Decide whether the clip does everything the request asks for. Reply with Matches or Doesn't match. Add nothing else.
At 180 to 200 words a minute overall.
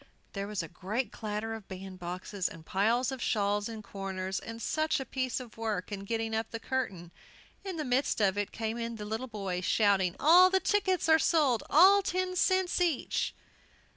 Matches